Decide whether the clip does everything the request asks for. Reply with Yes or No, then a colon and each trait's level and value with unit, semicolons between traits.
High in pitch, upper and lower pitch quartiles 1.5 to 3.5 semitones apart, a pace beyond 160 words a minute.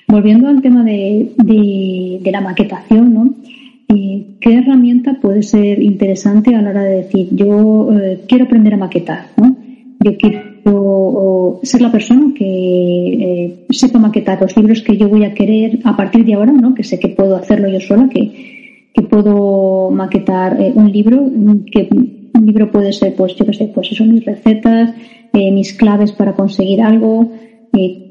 Yes: high, 215 Hz; average, 2.8 semitones; average, 175 wpm